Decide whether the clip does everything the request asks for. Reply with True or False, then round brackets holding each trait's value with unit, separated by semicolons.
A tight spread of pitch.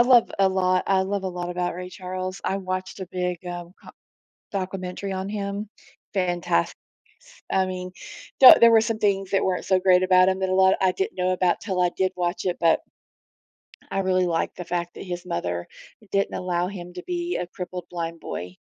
True (1.4 semitones)